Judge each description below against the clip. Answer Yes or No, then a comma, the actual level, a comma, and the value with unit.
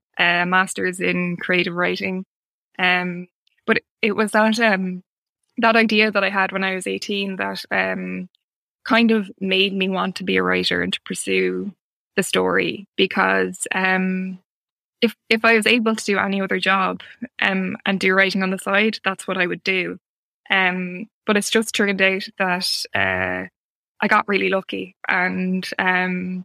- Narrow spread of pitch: Yes, narrow, 2.1 semitones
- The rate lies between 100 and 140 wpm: No, average, 170 wpm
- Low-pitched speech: No, high, 190 Hz